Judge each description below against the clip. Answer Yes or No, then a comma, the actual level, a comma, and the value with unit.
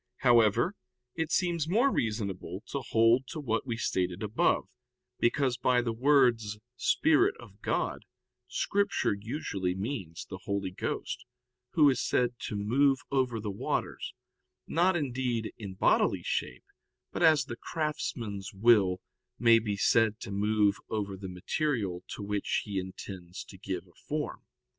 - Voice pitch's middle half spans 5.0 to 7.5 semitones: Yes, wide, 5.4 semitones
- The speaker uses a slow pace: No, average, 145 wpm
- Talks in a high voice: No, low, 115 Hz